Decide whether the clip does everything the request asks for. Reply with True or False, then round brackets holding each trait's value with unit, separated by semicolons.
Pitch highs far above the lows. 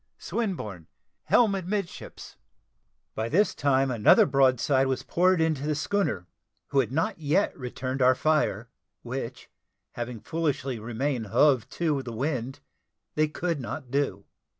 False (4.5 semitones)